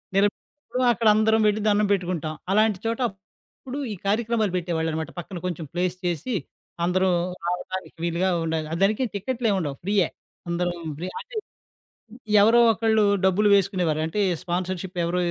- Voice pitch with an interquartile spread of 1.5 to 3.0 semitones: No, average, 3.7 semitones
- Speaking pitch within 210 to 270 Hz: No, high, 190 Hz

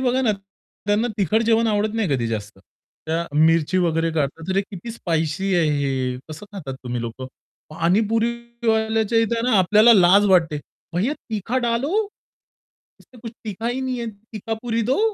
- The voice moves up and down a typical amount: No, wide, 5.9 semitones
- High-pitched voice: Yes, high, 205 Hz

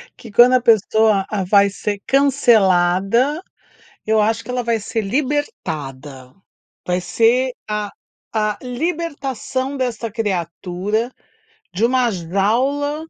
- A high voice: Yes, high, 225 Hz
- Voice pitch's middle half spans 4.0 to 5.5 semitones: Yes, average, 4.6 semitones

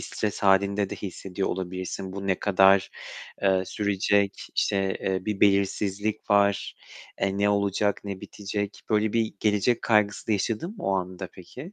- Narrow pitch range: Yes, narrow, 1.4 semitones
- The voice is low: Yes, low, 100 Hz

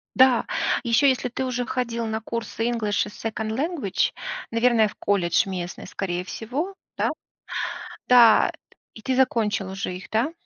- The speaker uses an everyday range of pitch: Yes, average, 3.3 semitones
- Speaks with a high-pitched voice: Yes, high, 230 Hz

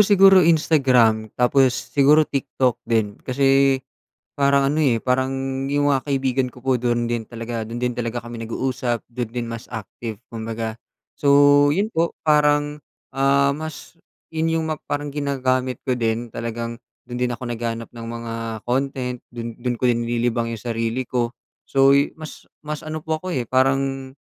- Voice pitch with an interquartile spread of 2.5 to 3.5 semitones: Yes, average, 3.2 semitones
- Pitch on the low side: Yes, low, 130 Hz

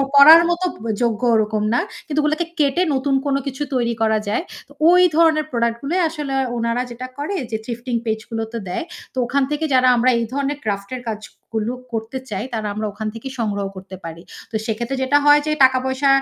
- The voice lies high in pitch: Yes, high, 245 Hz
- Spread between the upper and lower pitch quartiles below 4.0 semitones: No, average, 4.3 semitones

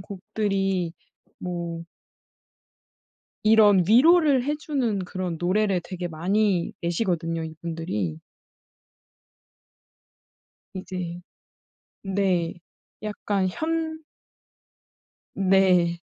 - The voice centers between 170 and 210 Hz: Yes, high, 190 Hz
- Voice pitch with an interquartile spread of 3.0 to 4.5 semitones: Yes, average, 3.7 semitones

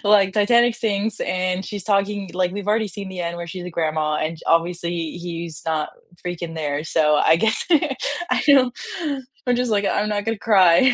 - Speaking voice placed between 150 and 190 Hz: Yes, medium, 185 Hz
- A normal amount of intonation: Yes, average, 4.1 semitones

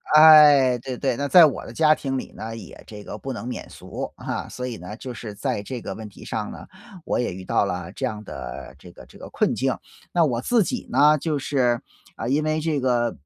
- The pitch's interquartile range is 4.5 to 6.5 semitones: Yes, average, 5.1 semitones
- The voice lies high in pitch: No, low, 125 Hz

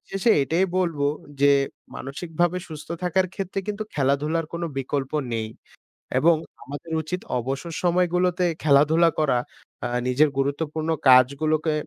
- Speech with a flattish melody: No, average, 3.7 semitones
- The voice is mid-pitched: Yes, medium, 155 Hz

